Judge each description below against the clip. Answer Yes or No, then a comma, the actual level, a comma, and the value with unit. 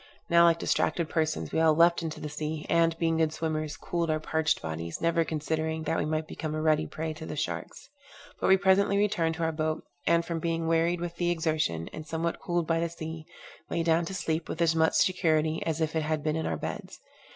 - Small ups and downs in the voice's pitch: Yes, narrow, 1.2 semitones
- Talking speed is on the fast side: Yes, fast, 230 wpm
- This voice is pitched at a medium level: Yes, medium, 160 Hz